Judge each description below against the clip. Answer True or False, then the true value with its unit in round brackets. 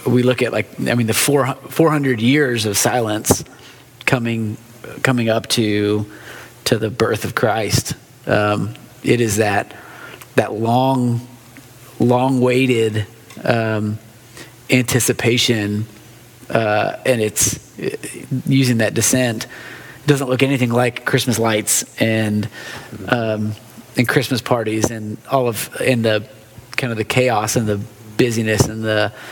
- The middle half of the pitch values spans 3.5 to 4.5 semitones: False (2.7 semitones)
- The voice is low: True (120 Hz)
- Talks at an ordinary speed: False (130 wpm)